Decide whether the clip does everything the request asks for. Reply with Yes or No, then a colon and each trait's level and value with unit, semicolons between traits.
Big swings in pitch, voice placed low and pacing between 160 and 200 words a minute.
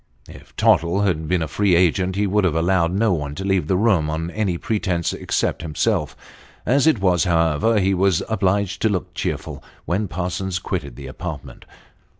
No: average, 3.3 semitones; very low, 90 Hz; average, 180 wpm